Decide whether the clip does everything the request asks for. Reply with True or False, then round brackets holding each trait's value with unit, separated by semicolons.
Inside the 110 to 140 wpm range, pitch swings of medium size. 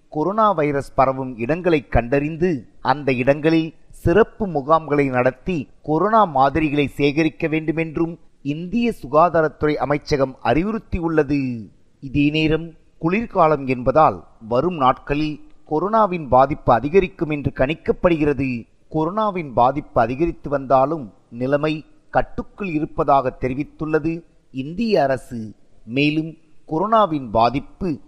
False (90 wpm; 3.2 semitones)